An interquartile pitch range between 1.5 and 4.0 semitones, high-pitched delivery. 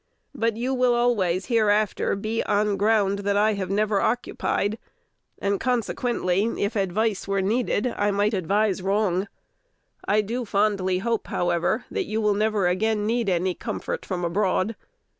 Yes: narrow, 2.4 semitones; high, 205 Hz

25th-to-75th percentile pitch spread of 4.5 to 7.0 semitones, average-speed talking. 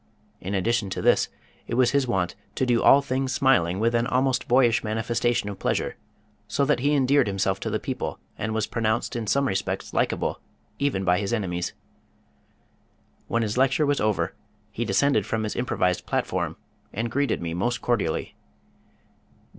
Yes: average, 4.9 semitones; average, 170 wpm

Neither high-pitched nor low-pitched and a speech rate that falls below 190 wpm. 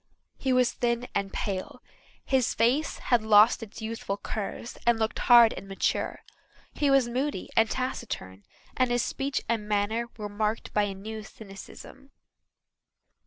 No: high, 225 Hz; average, 150 wpm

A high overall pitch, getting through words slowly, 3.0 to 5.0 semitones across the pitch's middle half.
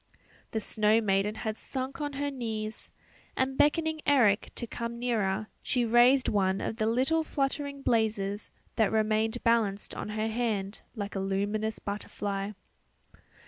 No: high, 220 Hz; average, 145 wpm; average, 3.5 semitones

